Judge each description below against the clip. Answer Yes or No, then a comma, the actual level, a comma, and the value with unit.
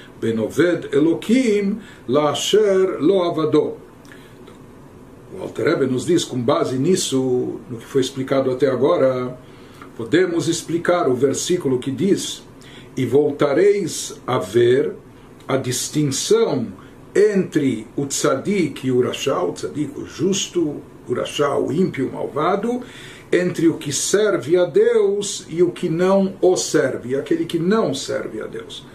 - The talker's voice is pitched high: No, medium, 165 Hz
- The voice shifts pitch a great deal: Yes, wide, 6.5 semitones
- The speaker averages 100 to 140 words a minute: Yes, average, 130 wpm